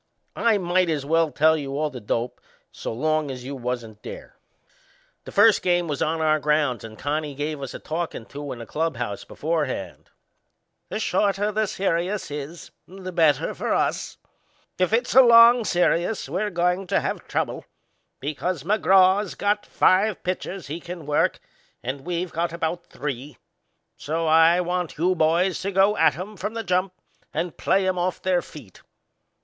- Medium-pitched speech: Yes, medium, 170 Hz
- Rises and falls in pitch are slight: No, average, 4.1 semitones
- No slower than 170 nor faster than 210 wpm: Yes, average, 175 wpm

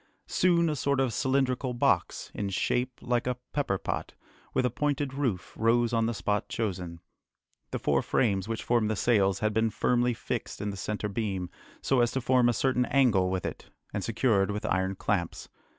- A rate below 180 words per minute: No, average, 185 wpm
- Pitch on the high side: No, low, 115 Hz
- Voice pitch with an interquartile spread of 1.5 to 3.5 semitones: No, average, 4.0 semitones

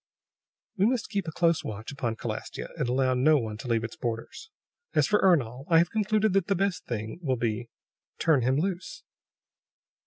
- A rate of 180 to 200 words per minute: Yes, average, 185 wpm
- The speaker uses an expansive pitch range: Yes, wide, 8.3 semitones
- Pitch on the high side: No, medium, 145 Hz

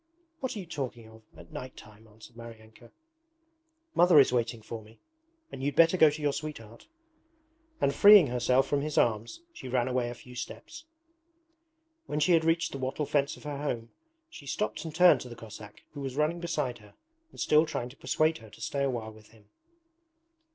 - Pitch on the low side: Yes, low, 130 Hz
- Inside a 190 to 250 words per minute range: Yes, average, 200 wpm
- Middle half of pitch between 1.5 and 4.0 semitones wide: No, average, 5.1 semitones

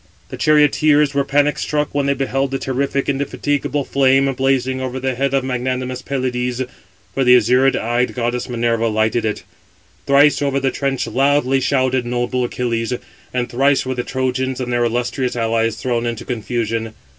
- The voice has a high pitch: No, low, 130 Hz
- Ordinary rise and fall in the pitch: No, narrow, 2.1 semitones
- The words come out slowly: No, average, 165 wpm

